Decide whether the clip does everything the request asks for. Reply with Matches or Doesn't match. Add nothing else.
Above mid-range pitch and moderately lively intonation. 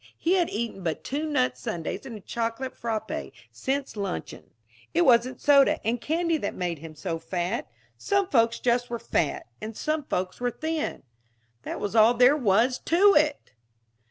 Doesn't match